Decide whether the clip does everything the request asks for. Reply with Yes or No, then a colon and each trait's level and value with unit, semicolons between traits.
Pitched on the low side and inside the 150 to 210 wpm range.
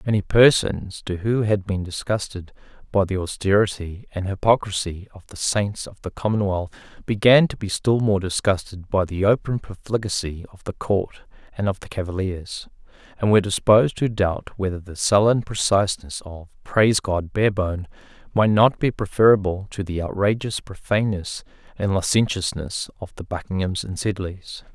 Yes: low, 100 Hz; average, 155 wpm